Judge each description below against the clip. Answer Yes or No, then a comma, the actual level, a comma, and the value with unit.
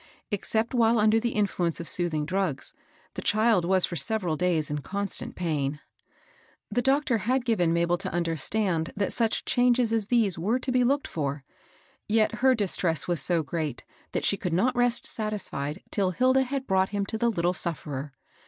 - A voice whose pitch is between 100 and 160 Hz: No, high, 195 Hz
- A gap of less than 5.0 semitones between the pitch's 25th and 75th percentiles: No, wide, 5.5 semitones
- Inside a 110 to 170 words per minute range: No, average, 185 wpm